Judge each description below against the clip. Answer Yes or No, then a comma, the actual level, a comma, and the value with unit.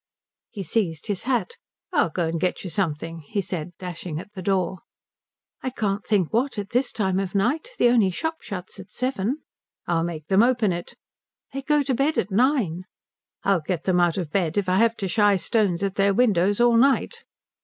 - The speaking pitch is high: Yes, high, 195 Hz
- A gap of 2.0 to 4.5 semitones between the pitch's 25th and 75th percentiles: No, average, 5.0 semitones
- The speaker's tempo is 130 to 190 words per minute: No, fast, 205 wpm